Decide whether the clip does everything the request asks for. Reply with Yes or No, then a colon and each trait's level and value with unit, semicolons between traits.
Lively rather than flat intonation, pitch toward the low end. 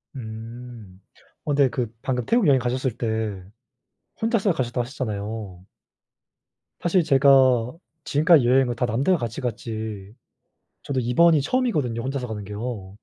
No: average, 4.0 semitones; low, 125 Hz